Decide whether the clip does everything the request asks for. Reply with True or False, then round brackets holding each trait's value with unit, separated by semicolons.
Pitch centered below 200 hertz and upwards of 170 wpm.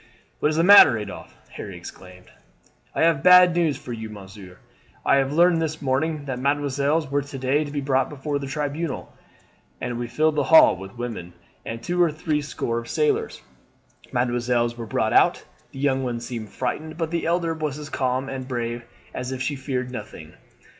True (135 Hz; 190 wpm)